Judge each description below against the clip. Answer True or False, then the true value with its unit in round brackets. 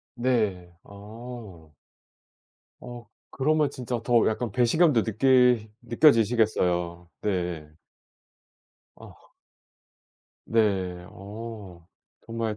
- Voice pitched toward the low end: True (110 Hz)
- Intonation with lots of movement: False (4.7 semitones)